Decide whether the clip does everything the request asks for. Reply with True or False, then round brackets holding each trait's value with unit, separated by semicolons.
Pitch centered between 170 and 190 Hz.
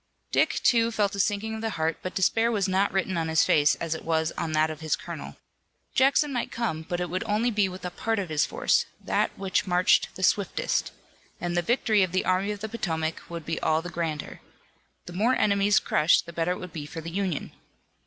True (185 Hz)